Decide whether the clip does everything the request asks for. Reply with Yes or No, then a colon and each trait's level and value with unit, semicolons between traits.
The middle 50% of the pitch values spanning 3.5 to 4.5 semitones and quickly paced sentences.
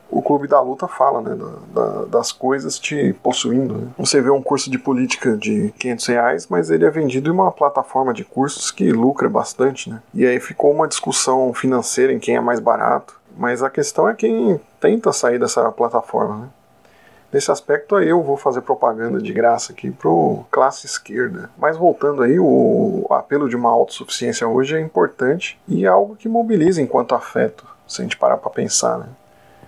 No: average, 4.9 semitones; fast, 190 wpm